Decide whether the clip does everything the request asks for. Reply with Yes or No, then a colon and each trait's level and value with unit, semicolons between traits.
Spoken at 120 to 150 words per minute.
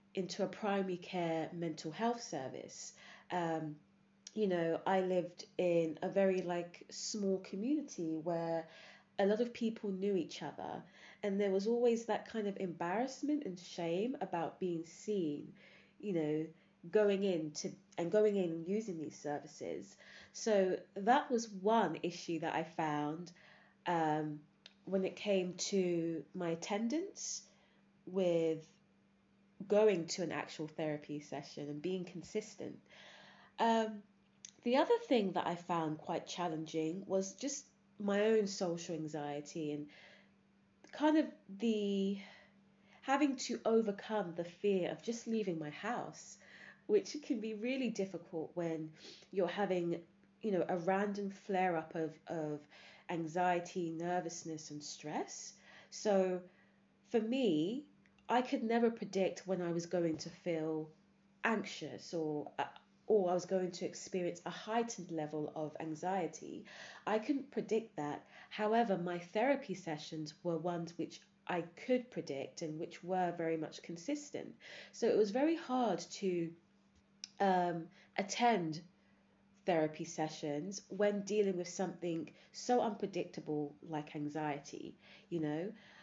Yes: slow, 135 wpm